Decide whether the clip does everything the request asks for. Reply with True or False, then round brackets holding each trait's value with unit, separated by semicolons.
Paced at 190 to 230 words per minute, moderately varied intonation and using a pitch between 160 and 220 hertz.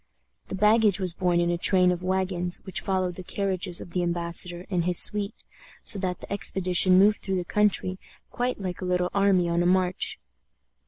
False (195 wpm; 1.7 semitones; 185 Hz)